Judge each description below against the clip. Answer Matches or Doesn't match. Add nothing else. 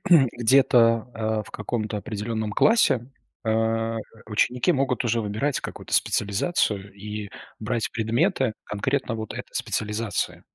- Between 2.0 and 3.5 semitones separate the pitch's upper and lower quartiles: Matches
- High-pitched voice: Doesn't match